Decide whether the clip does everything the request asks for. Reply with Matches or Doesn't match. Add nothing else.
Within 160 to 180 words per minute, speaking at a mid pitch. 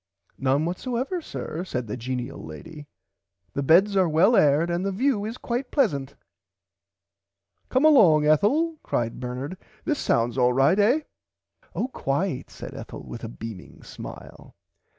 Doesn't match